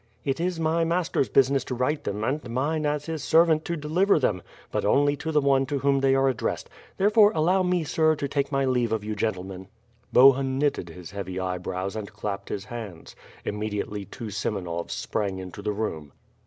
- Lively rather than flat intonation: Yes, wide, 6.9 semitones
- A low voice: Yes, low, 130 Hz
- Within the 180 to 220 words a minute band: Yes, average, 195 wpm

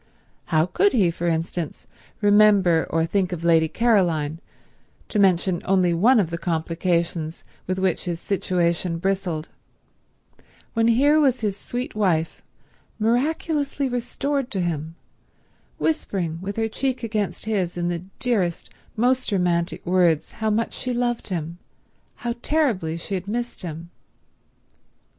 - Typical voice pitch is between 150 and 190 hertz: Yes, medium, 185 Hz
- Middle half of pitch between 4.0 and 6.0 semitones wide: Yes, average, 5.3 semitones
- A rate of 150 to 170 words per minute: No, slow, 135 wpm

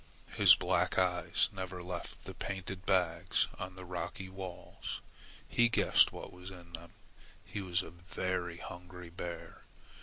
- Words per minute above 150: No, average, 145 wpm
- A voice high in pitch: No, very low, 90 Hz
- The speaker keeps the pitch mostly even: Yes, narrow, 1.2 semitones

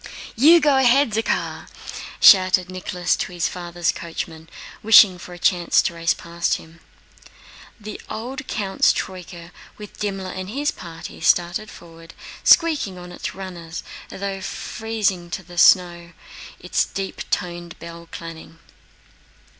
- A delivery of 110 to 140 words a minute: Yes, slow, 135 wpm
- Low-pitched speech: No, medium, 180 Hz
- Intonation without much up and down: No, average, 3.4 semitones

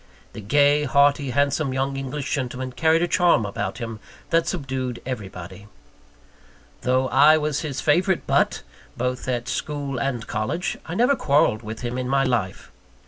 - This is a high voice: No, low, 135 Hz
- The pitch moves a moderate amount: Yes, average, 3.3 semitones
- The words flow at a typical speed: Yes, average, 155 wpm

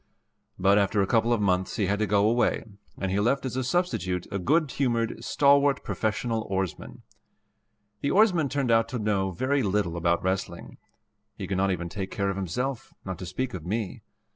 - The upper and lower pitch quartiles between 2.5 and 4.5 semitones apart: No, average, 5.1 semitones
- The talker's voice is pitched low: Yes, low, 105 Hz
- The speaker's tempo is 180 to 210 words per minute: Yes, average, 190 wpm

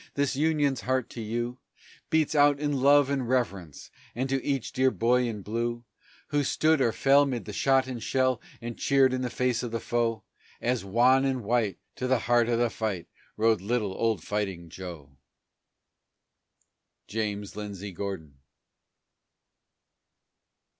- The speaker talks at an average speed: Yes, average, 155 wpm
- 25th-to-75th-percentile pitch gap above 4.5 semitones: No, average, 3.8 semitones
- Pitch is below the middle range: Yes, low, 120 Hz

